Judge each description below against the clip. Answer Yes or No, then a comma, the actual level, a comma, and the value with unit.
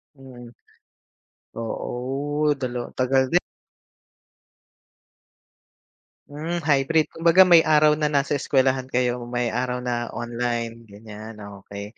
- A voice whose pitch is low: Yes, low, 130 Hz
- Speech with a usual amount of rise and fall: Yes, average, 3.5 semitones